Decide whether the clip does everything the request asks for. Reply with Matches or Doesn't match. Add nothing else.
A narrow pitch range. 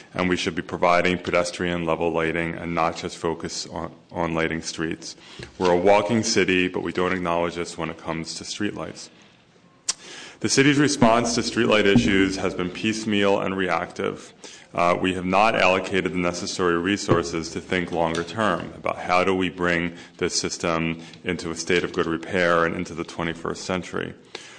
Matches